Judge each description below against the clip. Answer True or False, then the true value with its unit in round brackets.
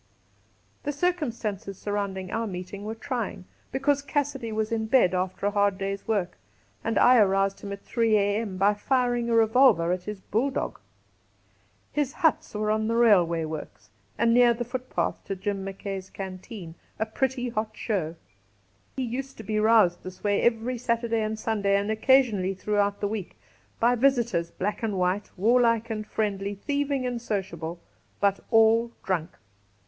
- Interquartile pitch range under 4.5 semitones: True (3.3 semitones)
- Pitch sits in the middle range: False (215 Hz)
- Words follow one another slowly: False (160 wpm)